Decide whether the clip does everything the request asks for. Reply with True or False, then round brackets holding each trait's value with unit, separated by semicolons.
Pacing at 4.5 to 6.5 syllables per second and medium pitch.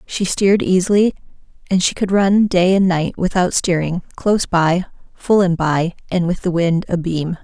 True (4.7 syllables/s; 180 Hz)